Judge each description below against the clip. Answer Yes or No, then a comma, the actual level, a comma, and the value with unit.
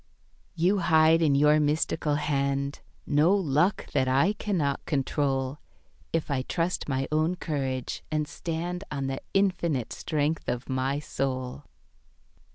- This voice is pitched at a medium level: Yes, medium, 150 Hz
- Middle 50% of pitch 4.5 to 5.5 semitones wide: No, average, 3.2 semitones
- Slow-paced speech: Yes, slow, 130 wpm